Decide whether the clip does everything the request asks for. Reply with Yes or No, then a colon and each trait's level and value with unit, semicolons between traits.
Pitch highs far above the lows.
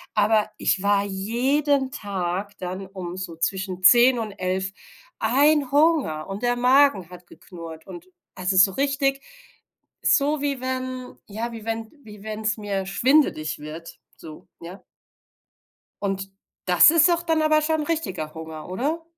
Yes: wide, 6.7 semitones